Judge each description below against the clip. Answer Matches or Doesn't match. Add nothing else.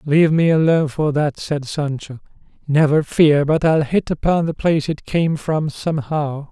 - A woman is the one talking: Doesn't match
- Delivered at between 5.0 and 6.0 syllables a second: Doesn't match